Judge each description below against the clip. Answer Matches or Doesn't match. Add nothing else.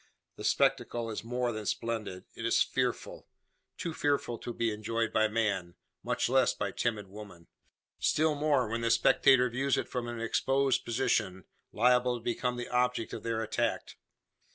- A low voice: Matches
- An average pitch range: Doesn't match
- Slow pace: Doesn't match